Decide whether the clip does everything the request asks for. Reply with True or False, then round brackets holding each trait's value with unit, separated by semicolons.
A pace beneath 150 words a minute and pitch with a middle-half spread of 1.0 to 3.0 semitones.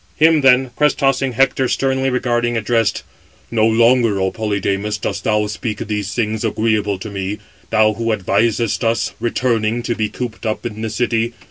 False (165 wpm; 2.4 semitones)